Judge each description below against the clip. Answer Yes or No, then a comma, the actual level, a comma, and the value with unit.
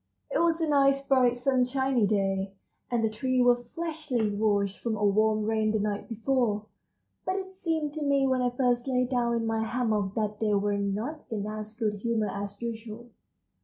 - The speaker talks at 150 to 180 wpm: No, average, 190 wpm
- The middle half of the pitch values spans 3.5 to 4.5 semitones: Yes, average, 3.8 semitones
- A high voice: Yes, high, 230 Hz